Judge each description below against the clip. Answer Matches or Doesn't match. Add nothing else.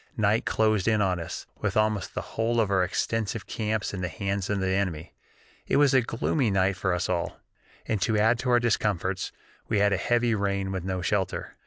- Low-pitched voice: Matches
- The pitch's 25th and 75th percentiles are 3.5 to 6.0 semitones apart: Doesn't match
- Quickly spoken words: Matches